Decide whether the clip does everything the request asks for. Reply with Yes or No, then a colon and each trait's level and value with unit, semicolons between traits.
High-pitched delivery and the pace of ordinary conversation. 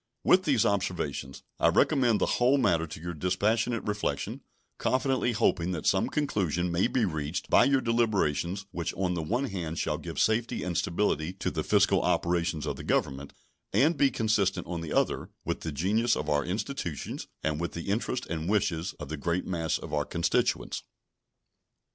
No: very low, 90 Hz; average, 180 wpm